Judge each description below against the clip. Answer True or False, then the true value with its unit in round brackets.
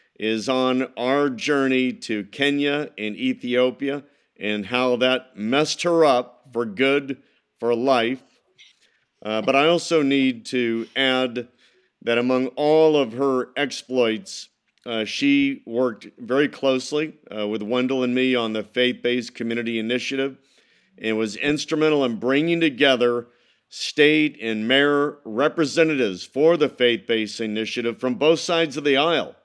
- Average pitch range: True (3.4 semitones)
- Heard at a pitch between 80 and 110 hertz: False (130 Hz)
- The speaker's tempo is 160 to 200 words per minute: False (140 wpm)